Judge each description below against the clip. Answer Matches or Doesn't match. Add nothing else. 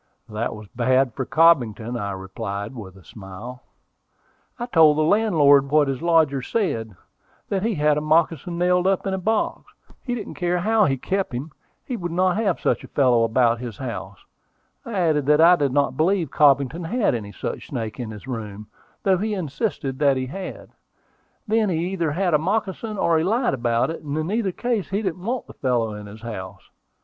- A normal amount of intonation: Doesn't match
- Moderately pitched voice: Matches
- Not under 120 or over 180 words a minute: Doesn't match